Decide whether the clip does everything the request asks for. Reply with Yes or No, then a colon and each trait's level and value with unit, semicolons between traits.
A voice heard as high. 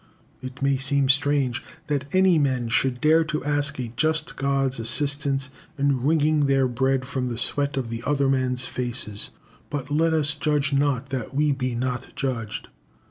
No: low, 135 Hz